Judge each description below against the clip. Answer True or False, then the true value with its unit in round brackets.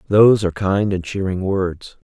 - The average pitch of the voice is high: False (95 Hz)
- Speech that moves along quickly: False (170 wpm)